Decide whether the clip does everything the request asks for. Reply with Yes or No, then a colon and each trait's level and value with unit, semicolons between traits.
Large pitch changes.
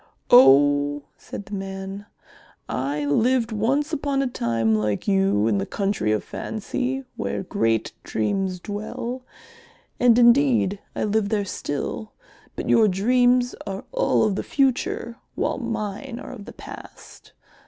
Yes: wide, 8.5 semitones